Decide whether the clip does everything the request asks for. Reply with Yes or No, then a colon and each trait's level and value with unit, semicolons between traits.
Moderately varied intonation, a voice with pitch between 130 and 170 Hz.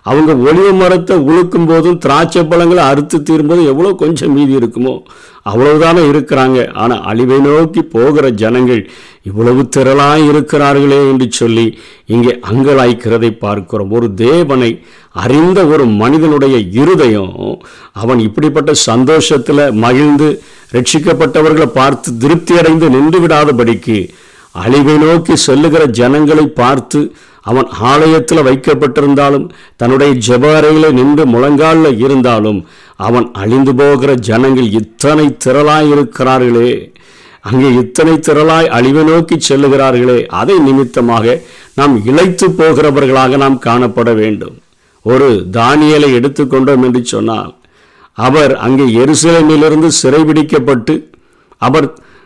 Yes: average, 4.0 semitones; medium, 140 Hz